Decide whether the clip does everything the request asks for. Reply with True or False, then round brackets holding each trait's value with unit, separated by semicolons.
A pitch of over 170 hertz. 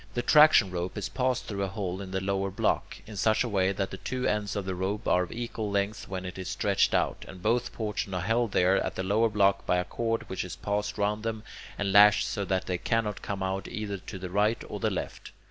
False (100 Hz)